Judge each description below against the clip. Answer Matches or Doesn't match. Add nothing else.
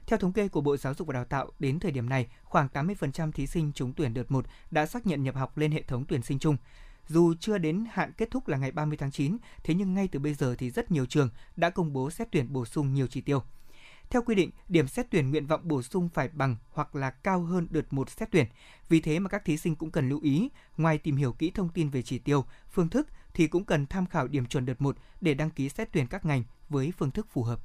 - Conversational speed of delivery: Doesn't match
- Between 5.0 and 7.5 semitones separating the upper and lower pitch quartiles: Doesn't match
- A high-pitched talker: Doesn't match